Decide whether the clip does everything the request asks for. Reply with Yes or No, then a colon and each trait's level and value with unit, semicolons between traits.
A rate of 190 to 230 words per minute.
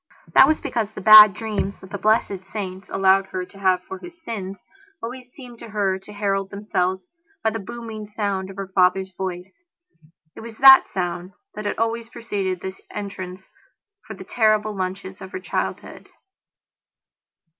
No: average, 165 wpm